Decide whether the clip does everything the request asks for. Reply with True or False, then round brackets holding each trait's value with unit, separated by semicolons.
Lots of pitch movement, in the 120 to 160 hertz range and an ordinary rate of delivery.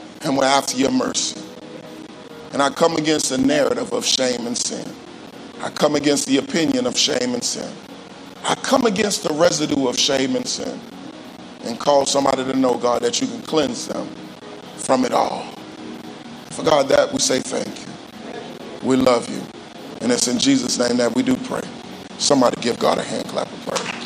True (5.9 semitones; 135 Hz; 185 wpm)